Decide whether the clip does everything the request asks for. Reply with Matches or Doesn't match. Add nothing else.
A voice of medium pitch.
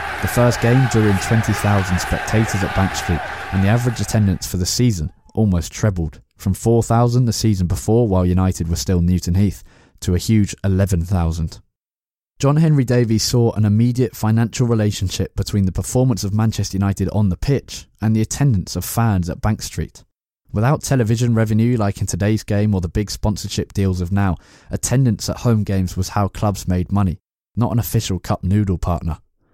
Doesn't match